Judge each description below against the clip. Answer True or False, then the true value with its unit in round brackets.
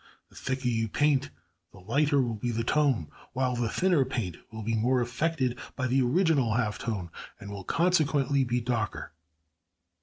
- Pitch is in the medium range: False (125 Hz)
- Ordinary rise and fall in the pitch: True (3.9 semitones)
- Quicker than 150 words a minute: True (170 wpm)